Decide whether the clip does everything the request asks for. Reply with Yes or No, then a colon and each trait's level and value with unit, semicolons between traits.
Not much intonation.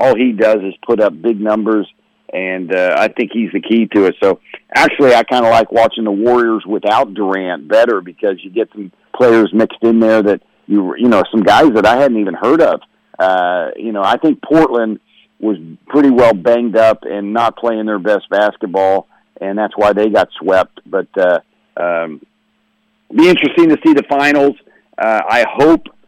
No: average, 3.3 semitones